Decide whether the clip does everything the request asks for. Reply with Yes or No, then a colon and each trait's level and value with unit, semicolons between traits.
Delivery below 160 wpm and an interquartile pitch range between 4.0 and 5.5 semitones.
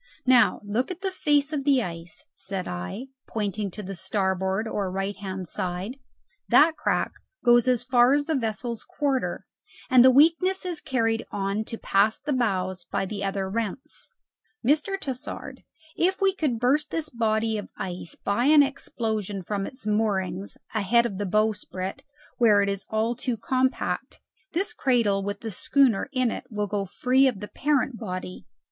No: average, 170 wpm; average, 5.0 semitones